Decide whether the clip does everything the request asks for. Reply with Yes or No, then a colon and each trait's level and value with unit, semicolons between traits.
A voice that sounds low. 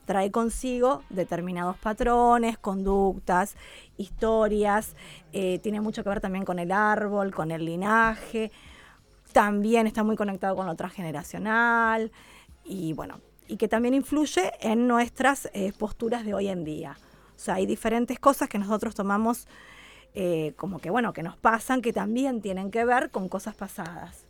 No: high, 210 Hz